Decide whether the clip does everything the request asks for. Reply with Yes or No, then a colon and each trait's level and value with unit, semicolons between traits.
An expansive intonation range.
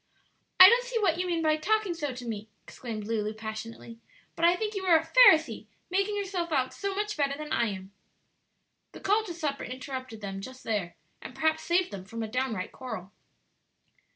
Yes: wide, 8.3 semitones